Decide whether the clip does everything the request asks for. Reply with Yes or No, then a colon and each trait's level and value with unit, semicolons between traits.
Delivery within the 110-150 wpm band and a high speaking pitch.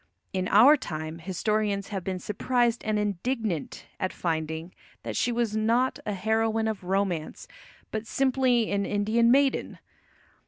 Yes: slow, 135 wpm; high, 210 Hz